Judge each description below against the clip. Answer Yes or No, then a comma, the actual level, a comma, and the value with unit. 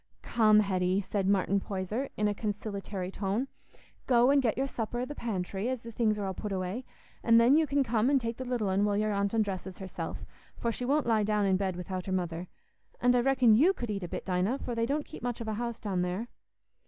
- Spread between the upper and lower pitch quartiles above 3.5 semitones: Yes, average, 3.9 semitones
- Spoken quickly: Yes, fast, 240 wpm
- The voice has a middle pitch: No, high, 215 Hz